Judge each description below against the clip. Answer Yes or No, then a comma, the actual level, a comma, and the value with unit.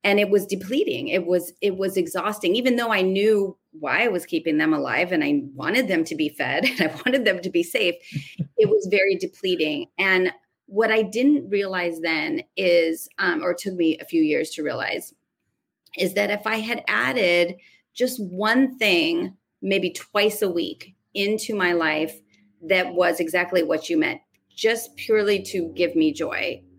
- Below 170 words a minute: No, average, 180 wpm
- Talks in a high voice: Yes, high, 195 Hz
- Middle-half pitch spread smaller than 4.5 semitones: No, average, 4.9 semitones